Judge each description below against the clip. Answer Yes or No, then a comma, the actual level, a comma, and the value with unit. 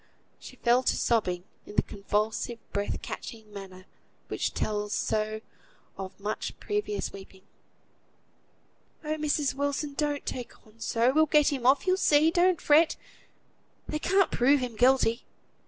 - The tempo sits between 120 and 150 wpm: Yes, average, 140 wpm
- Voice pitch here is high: Yes, very high, 250 Hz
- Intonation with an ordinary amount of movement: No, wide, 5.9 semitones